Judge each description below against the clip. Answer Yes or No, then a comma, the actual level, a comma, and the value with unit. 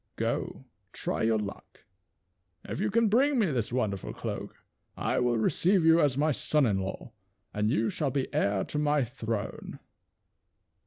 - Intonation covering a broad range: Yes, wide, 6.7 semitones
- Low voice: Yes, low, 130 Hz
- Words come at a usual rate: Yes, average, 165 wpm